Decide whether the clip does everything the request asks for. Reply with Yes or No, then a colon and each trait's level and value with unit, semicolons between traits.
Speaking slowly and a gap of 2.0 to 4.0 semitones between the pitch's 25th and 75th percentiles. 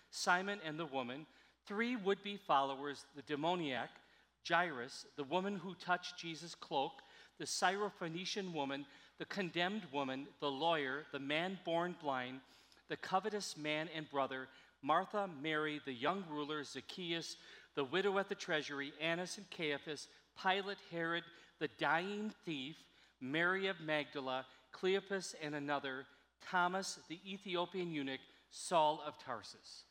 No: slow, 130 wpm; average, 4.5 semitones